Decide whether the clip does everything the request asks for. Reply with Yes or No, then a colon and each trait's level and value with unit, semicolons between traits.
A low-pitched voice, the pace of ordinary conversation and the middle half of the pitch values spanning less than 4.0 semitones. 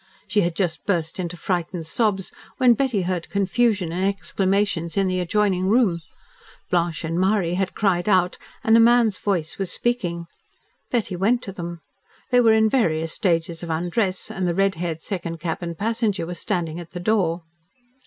No: medium, 185 Hz; average, 175 wpm; average, 3.5 semitones